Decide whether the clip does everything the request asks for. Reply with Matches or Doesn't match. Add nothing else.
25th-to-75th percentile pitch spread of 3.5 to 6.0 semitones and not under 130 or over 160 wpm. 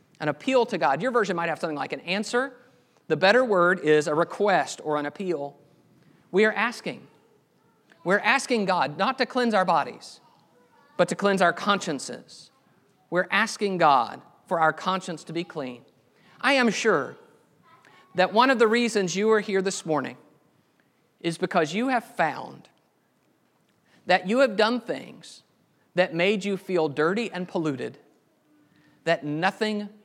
Matches